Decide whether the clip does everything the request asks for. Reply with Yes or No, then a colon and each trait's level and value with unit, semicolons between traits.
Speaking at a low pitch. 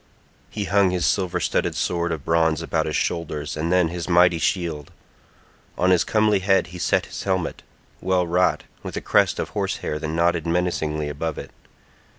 Yes: very low, 85 Hz